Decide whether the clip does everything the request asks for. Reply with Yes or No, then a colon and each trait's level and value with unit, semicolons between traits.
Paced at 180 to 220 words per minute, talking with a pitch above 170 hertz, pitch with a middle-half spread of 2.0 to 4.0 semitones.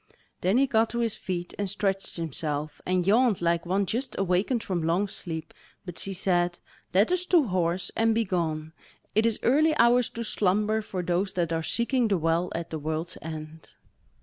No: average, 185 wpm; medium, 185 Hz; average, 4.7 semitones